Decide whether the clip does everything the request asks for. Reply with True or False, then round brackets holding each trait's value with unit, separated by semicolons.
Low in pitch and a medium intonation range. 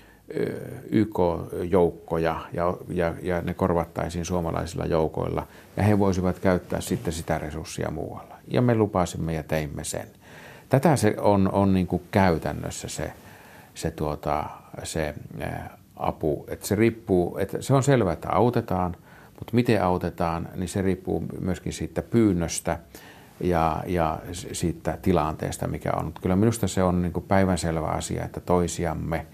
True (90 Hz; 3.1 semitones)